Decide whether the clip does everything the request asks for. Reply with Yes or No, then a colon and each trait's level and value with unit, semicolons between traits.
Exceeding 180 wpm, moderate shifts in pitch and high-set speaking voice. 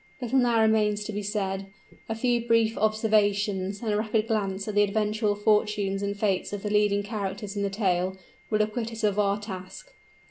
No: average, 190 wpm; narrow, 1.5 semitones; high, 210 Hz